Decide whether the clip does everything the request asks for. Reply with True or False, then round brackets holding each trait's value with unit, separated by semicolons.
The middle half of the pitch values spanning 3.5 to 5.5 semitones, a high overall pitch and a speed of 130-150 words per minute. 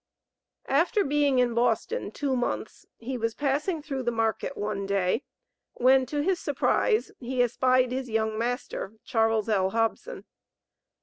True (3.8 semitones; 250 Hz; 140 wpm)